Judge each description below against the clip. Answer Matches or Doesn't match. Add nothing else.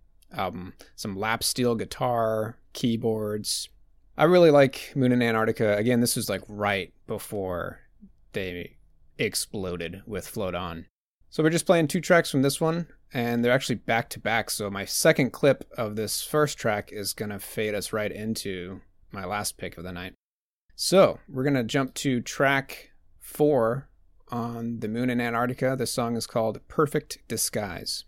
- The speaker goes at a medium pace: Matches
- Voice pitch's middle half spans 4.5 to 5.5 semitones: Matches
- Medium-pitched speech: Doesn't match